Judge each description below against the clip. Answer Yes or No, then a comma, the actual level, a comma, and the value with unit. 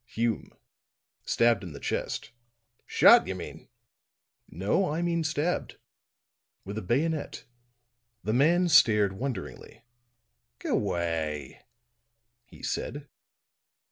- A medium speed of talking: No, slow, 95 wpm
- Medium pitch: No, low, 115 Hz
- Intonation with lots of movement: Yes, wide, 8.6 semitones